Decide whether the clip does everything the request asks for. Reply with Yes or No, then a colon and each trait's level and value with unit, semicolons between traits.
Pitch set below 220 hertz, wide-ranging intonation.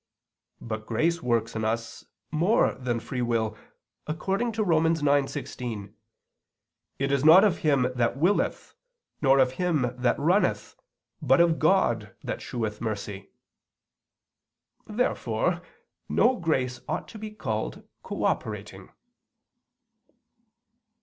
Yes: low, 135 Hz; wide, 6.4 semitones